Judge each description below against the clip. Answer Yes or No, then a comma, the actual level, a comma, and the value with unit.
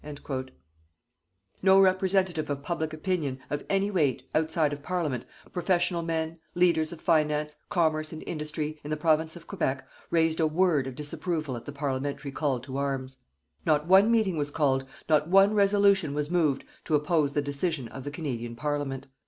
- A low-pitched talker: No, medium, 155 Hz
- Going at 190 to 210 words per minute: No, average, 170 wpm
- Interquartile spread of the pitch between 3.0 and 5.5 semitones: Yes, average, 3.4 semitones